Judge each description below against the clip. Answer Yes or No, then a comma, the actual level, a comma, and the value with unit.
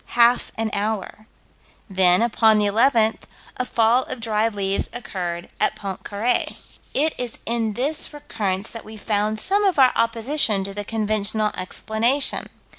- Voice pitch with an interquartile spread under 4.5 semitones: Yes, average, 2.8 semitones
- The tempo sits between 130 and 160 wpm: Yes, average, 145 wpm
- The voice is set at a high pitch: Yes, high, 220 Hz